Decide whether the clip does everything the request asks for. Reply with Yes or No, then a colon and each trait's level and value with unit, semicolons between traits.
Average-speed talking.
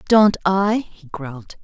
Yes: average, 145 wpm